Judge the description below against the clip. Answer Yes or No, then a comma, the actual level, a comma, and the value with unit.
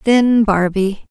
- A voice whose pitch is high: Yes, high, 210 Hz